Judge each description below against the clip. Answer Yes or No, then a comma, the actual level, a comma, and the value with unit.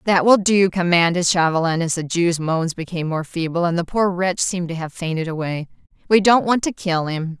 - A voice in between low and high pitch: Yes, medium, 175 Hz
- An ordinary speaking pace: No, fast, 220 wpm